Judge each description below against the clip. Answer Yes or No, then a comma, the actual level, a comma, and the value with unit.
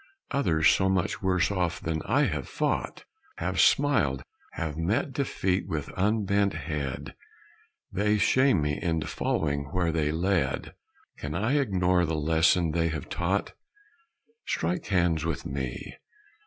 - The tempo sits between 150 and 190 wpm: No, slow, 135 wpm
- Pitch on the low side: Yes, very low, 85 Hz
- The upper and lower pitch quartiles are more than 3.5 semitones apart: Yes, average, 3.9 semitones